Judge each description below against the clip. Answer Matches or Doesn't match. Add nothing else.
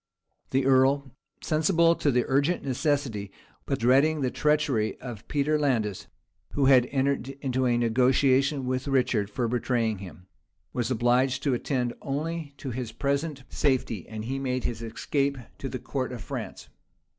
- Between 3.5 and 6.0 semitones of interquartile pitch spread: Doesn't match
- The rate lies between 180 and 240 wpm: Doesn't match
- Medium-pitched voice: Doesn't match